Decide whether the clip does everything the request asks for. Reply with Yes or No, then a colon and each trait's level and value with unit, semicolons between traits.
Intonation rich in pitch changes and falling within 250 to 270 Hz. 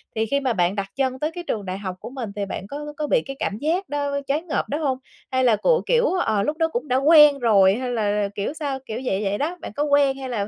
Yes: wide, 6.1 semitones; very high, 260 Hz